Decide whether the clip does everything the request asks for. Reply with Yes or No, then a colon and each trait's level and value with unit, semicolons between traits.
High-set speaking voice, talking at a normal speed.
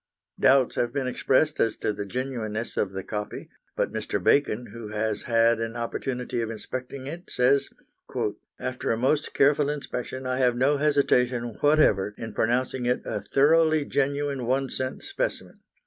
No: low, 130 Hz; average, 160 wpm